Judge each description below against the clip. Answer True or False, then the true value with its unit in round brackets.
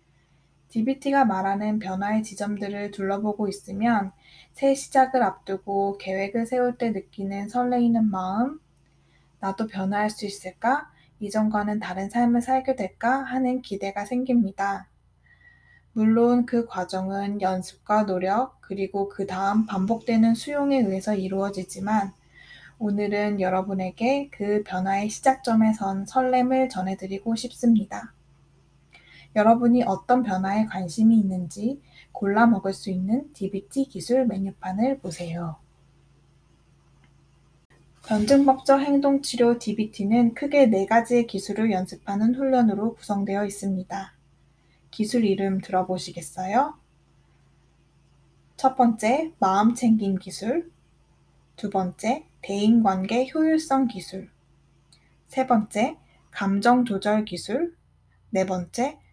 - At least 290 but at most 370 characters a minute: False (255 characters per minute)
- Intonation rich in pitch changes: False (3.9 semitones)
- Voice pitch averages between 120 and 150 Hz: False (210 Hz)